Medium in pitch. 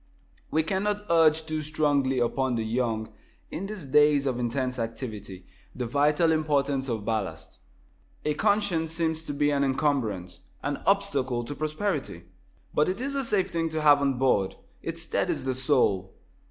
Yes: medium, 145 Hz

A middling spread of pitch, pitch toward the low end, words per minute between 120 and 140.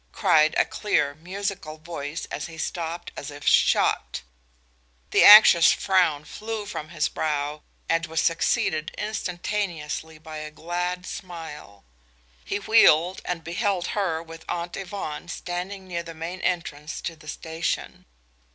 No: average, 3.0 semitones; medium, 170 Hz; slow, 135 wpm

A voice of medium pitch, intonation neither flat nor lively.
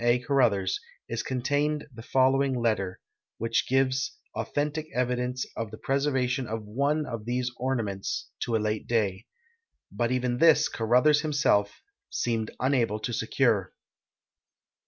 No: low, 125 Hz; average, 3.1 semitones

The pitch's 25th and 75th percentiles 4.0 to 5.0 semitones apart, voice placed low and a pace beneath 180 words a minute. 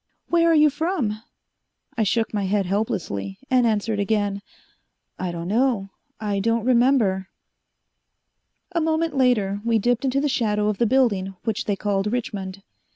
No: average, 4.3 semitones; high, 215 Hz; average, 155 wpm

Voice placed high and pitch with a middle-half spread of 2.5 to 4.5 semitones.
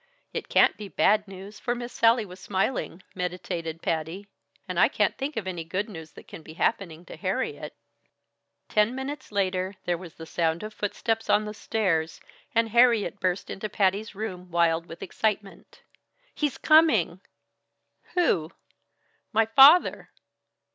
Yes: high, 200 Hz; average, 4.2 semitones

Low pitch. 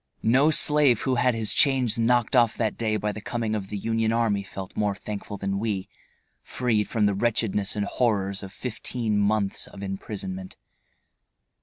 Yes: low, 110 Hz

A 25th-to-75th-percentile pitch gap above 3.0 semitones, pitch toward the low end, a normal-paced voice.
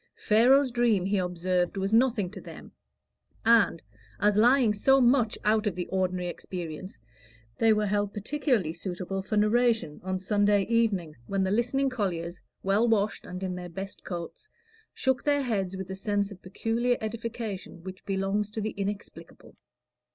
No: average, 3.6 semitones; high, 205 Hz; average, 155 wpm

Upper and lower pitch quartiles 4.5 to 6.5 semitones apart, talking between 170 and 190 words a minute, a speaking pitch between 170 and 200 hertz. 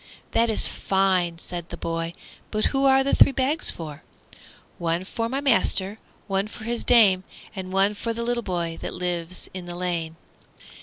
Yes: average, 5.0 semitones; average, 175 wpm; high, 190 Hz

